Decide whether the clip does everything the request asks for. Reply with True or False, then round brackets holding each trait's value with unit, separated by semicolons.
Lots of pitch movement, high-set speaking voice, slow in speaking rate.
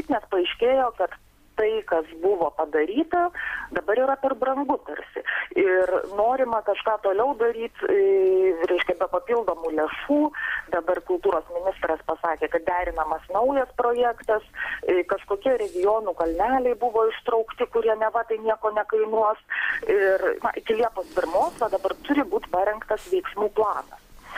True (6.1 semitones; 220 Hz; 125 wpm)